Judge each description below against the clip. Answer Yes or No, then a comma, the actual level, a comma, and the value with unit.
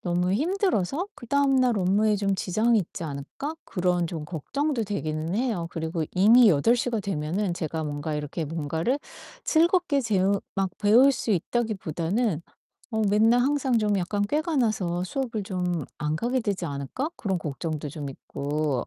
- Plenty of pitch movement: Yes, wide, 6.7 semitones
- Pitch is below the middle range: No, high, 195 Hz